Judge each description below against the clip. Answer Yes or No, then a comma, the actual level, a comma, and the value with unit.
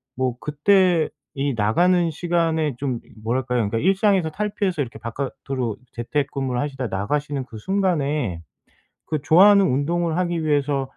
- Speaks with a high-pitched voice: No, medium, 145 Hz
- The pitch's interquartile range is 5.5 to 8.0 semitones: No, average, 5.1 semitones